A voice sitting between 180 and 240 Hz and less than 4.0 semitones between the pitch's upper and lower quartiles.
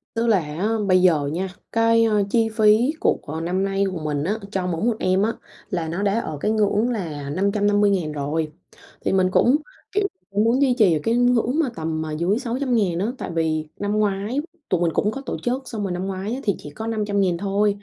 No: high, 200 Hz; average, 4.8 semitones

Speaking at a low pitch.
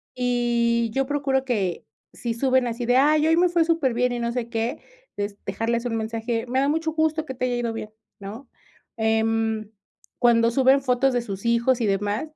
No: high, 240 Hz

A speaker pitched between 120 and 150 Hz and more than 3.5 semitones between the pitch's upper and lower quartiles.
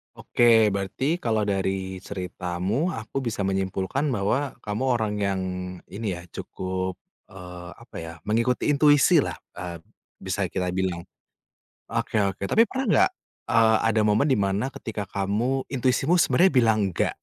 No: low, 105 Hz; average, 5.0 semitones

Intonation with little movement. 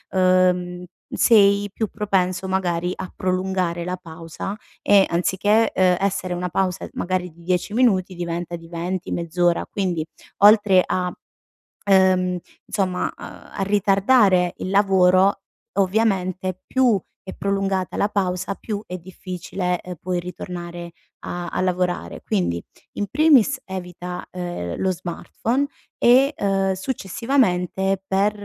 Yes: narrow, 1.8 semitones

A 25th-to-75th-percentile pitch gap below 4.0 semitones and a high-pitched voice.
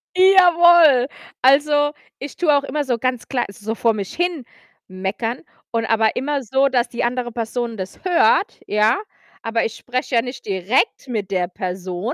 No: average, 4.6 semitones; high, 245 Hz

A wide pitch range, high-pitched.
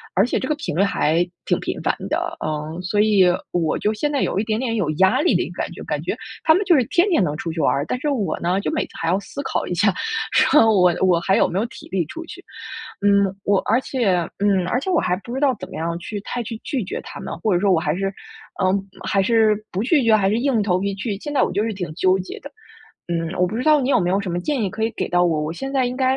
Yes: wide, 5.7 semitones; high, 200 Hz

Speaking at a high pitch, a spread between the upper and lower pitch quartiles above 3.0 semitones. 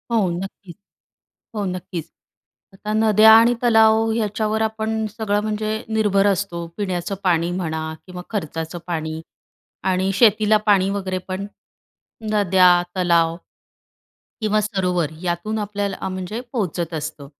Yes: high, 195 Hz; average, 3.5 semitones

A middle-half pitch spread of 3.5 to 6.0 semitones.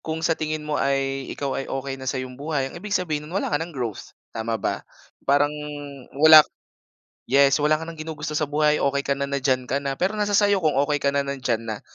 No: narrow, 2.5 semitones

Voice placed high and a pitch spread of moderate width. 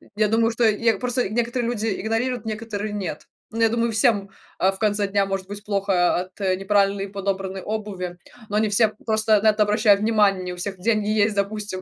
No: high, 210 Hz; narrow, 2.1 semitones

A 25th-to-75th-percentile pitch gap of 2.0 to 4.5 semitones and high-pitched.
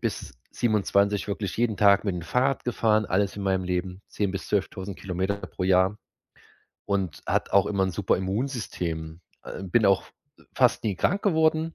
No: narrow, 2.5 semitones; low, 100 Hz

